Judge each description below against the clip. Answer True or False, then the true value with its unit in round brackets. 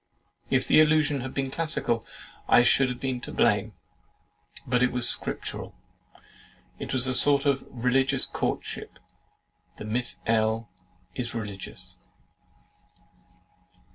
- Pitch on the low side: True (125 Hz)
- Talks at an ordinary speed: False (120 wpm)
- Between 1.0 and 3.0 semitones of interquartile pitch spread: True (2.7 semitones)